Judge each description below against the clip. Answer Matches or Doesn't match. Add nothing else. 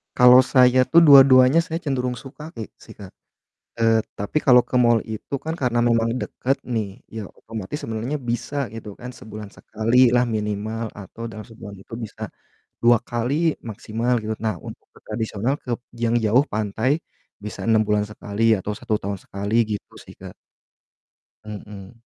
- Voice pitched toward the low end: Matches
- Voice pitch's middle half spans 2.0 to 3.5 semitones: Matches